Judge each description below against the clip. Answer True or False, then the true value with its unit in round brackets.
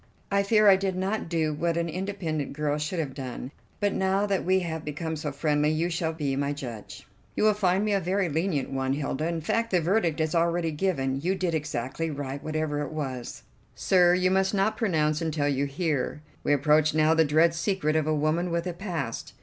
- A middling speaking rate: False (215 wpm)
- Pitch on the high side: False (160 Hz)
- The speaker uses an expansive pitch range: False (3.8 semitones)